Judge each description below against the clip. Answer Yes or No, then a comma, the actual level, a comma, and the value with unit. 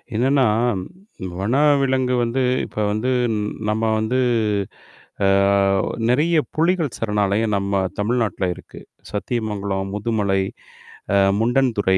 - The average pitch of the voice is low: Yes, low, 115 Hz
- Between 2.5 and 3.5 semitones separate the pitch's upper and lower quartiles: No, average, 4.1 semitones